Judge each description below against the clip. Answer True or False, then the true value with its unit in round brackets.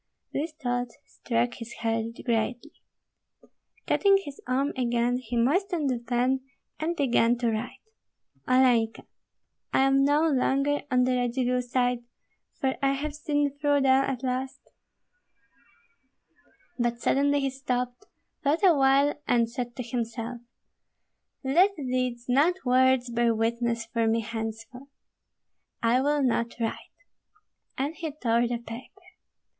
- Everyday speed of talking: False (130 wpm)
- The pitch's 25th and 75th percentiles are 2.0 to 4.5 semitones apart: True (2.8 semitones)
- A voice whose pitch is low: False (255 Hz)